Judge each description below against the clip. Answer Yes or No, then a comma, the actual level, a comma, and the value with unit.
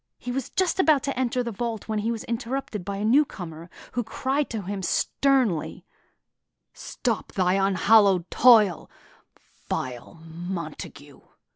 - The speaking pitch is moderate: No, high, 215 Hz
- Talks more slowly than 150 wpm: Yes, slow, 135 wpm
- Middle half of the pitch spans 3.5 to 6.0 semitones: Yes, wide, 5.4 semitones